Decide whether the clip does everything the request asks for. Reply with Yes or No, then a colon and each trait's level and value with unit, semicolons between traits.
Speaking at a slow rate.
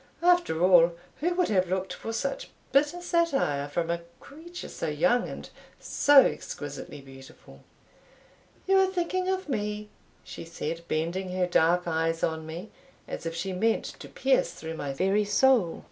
No: average, 160 wpm